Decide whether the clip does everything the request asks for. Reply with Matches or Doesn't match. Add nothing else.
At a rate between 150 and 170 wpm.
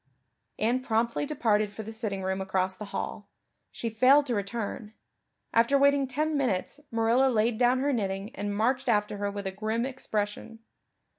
Matches